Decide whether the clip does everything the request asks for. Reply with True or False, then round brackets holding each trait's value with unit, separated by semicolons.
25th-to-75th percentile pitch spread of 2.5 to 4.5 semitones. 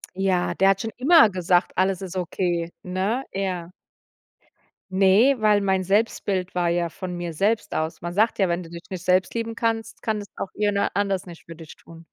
True (2.8 semitones)